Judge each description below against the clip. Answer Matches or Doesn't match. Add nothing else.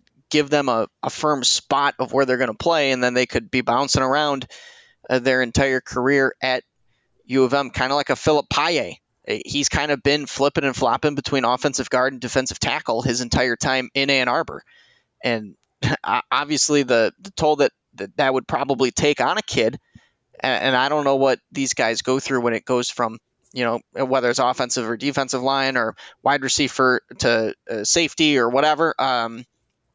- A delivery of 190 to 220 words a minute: Matches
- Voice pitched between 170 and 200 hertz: Doesn't match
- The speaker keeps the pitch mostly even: Matches